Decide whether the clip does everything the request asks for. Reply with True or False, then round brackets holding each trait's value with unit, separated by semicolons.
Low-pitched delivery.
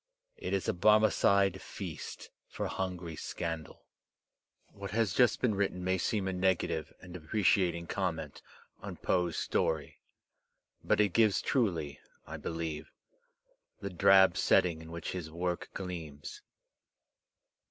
True (90 Hz)